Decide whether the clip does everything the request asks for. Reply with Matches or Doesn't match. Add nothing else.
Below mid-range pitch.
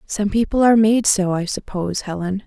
Doesn't match